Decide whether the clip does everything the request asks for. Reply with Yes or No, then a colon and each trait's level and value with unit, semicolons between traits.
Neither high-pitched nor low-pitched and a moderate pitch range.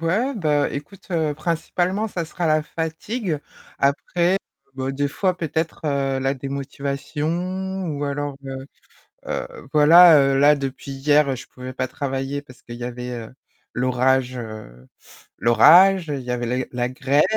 Yes: medium, 145 Hz; average, 4.0 semitones